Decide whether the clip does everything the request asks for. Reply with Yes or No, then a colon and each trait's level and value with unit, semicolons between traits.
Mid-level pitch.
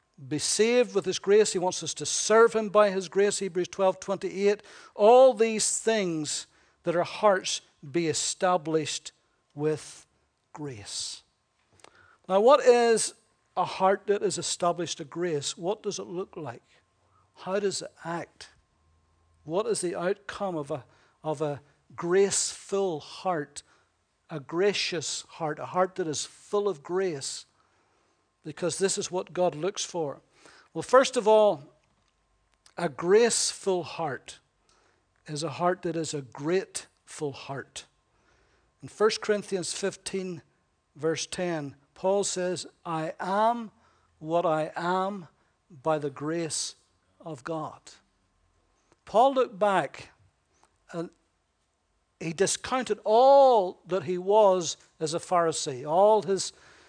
Yes: medium, 180 Hz